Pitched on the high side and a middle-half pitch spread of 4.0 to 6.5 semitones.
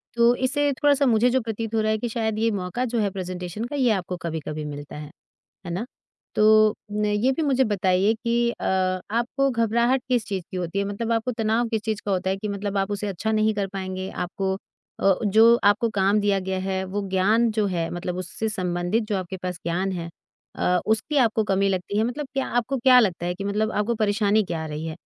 No: high, 210 Hz; average, 3.5 semitones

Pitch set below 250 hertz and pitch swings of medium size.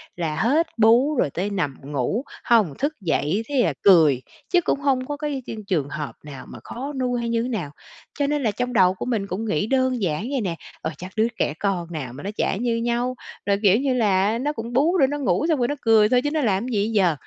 No: high, 225 Hz; wide, 5.9 semitones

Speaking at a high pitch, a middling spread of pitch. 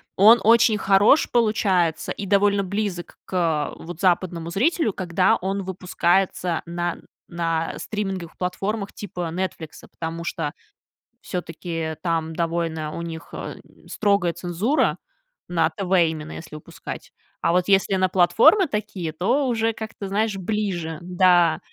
No: medium, 180 Hz; average, 3.3 semitones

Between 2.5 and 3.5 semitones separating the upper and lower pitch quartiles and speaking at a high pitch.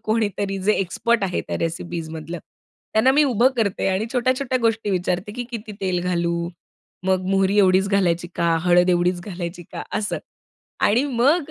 No: average, 4.1 semitones; high, 195 Hz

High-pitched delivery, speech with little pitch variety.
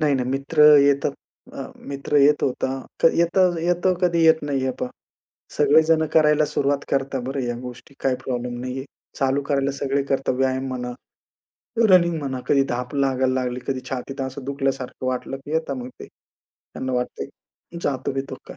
No: low, 135 Hz; narrow, 2.2 semitones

